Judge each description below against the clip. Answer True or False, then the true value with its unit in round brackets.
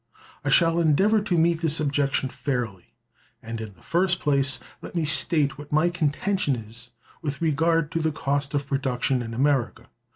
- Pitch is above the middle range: False (145 Hz)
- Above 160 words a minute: True (170 wpm)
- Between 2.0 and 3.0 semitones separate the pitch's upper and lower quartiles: False (3.6 semitones)